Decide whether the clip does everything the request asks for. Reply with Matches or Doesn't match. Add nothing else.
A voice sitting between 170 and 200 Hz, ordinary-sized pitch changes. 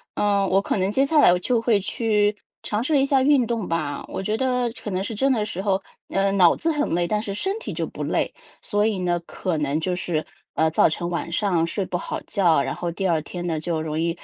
Matches